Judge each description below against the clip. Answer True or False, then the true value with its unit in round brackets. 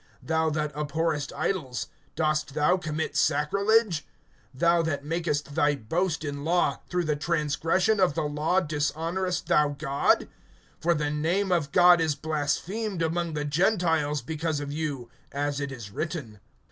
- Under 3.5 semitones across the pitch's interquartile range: True (2.8 semitones)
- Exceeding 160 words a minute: False (145 wpm)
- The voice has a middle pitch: True (155 Hz)